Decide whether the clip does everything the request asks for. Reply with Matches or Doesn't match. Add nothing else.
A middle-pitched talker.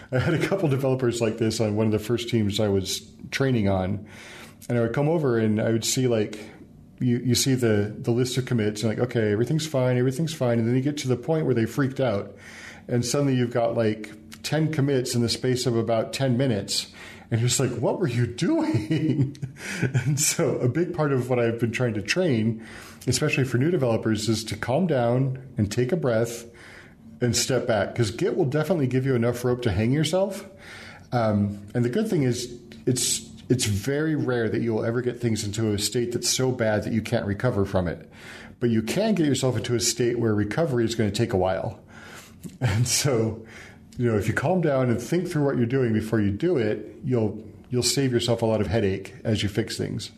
Doesn't match